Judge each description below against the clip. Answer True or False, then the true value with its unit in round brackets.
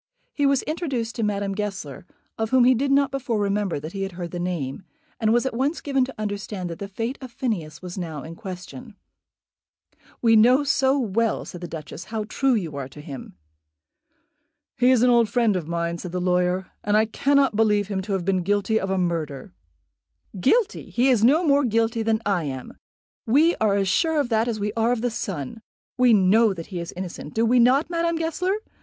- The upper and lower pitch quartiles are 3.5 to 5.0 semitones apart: False (5.5 semitones)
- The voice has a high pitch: True (215 Hz)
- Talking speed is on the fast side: True (210 wpm)